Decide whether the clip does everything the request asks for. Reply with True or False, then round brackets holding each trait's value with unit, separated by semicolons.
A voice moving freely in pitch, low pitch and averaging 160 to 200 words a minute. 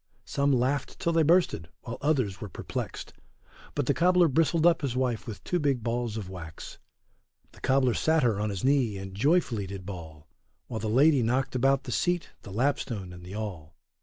True (6.2 semitones; 125 Hz; 190 wpm)